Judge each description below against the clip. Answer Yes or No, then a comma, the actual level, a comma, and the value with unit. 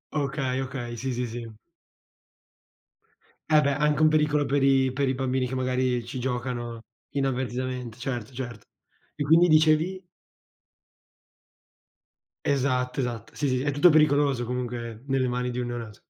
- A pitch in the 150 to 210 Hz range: No, low, 130 Hz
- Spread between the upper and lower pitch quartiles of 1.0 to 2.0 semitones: No, narrow, 2.5 semitones